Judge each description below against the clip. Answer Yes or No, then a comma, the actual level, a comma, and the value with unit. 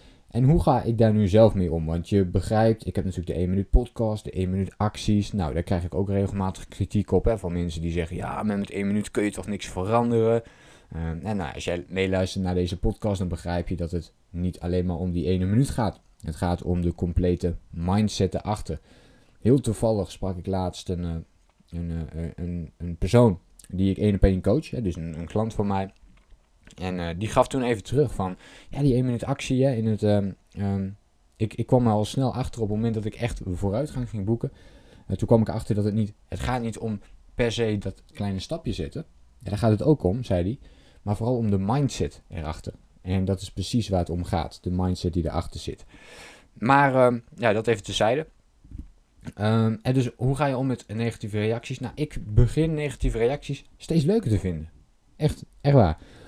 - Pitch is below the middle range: Yes, low, 100 Hz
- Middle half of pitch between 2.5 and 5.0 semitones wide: Yes, average, 4.4 semitones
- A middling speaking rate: No, fast, 215 wpm